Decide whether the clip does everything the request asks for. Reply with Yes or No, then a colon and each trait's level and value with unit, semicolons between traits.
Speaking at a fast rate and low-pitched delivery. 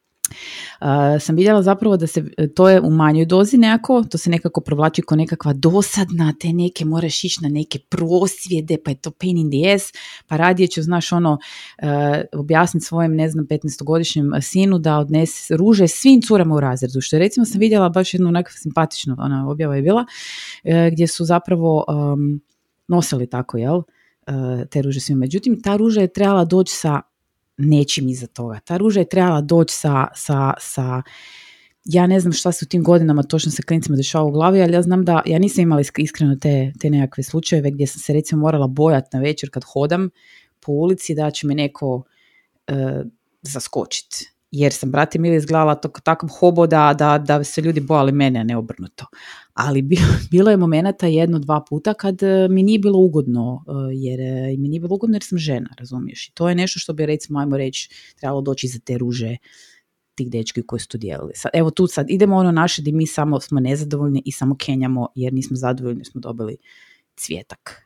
No: fast, 195 wpm; medium, 155 Hz